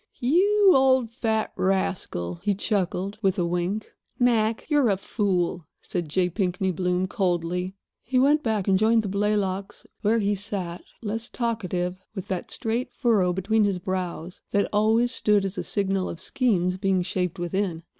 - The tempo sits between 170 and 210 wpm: No, average, 160 wpm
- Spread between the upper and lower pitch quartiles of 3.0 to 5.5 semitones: Yes, average, 3.5 semitones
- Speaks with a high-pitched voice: Yes, high, 195 Hz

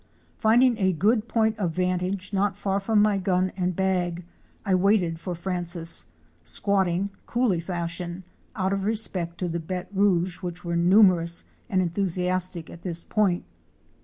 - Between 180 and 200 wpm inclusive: No, average, 155 wpm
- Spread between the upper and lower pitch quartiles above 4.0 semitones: No, narrow, 2.4 semitones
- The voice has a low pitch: No, medium, 185 Hz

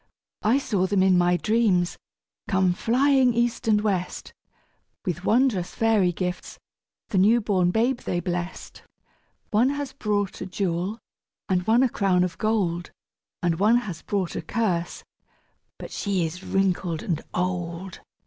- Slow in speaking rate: No, average, 145 wpm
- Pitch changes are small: No, average, 3.9 semitones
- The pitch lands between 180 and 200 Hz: Yes, high, 190 Hz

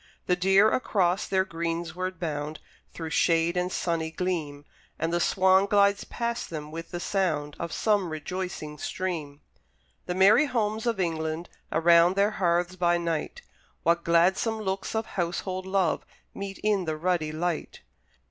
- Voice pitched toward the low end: No, medium, 175 Hz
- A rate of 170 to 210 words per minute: No, average, 145 wpm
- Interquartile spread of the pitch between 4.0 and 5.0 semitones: No, average, 2.8 semitones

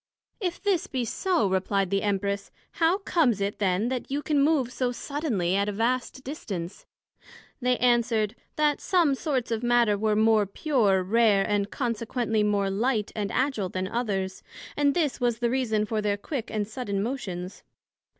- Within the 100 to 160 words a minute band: No, average, 170 wpm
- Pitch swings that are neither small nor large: Yes, average, 4.6 semitones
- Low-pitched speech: No, high, 225 Hz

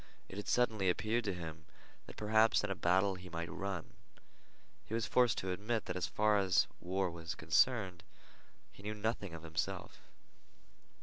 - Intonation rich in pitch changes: No, average, 3.5 semitones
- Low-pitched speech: Yes, very low, 95 Hz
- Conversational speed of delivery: Yes, average, 170 wpm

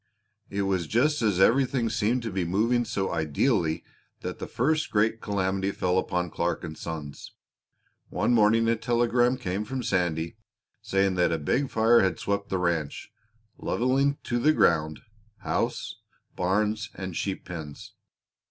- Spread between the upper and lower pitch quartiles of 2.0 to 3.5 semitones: No, average, 4.9 semitones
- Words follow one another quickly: No, average, 150 wpm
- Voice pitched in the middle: No, low, 100 Hz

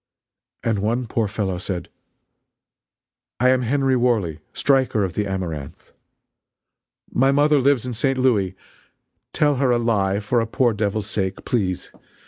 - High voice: No, low, 115 Hz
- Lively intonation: No, average, 4.7 semitones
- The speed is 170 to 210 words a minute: No, average, 140 wpm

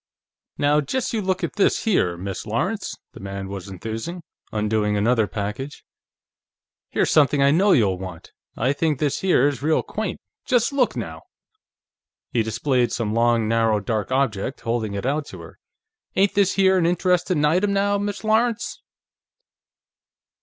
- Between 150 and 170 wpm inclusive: Yes, average, 155 wpm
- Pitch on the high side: No, medium, 140 Hz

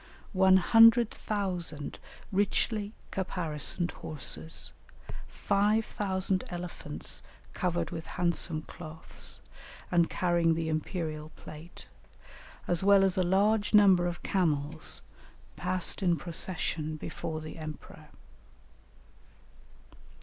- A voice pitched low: No, medium, 175 Hz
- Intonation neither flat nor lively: Yes, average, 3.3 semitones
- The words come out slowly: Yes, slow, 95 wpm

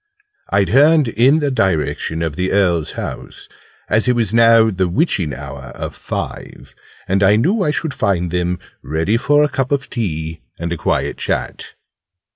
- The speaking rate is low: No, average, 170 wpm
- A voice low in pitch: Yes, low, 100 Hz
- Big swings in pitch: Yes, wide, 7.3 semitones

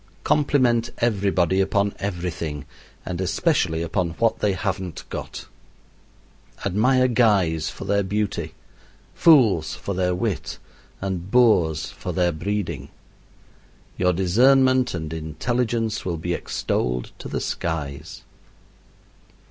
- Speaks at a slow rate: Yes, slow, 110 wpm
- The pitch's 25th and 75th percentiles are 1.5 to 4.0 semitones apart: No, average, 5.2 semitones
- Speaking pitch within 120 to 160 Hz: No, very low, 95 Hz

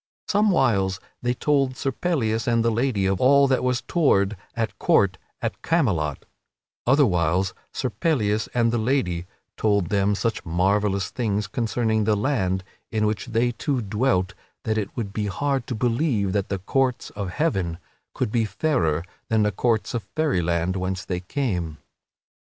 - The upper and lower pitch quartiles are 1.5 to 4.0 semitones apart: No, average, 4.8 semitones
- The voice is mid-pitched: No, low, 110 Hz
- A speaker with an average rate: Yes, average, 160 wpm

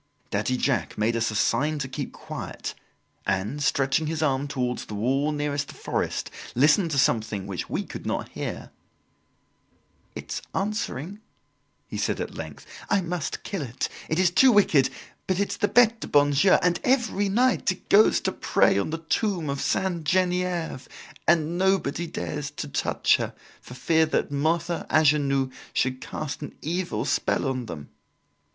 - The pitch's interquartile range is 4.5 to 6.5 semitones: Yes, average, 5.3 semitones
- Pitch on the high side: No, medium, 150 Hz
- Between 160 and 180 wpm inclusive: Yes, average, 165 wpm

